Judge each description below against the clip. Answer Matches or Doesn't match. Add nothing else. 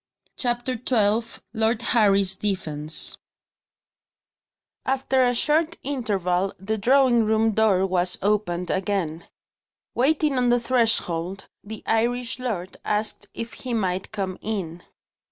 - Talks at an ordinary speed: Doesn't match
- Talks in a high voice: Matches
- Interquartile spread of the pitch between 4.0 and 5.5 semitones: Matches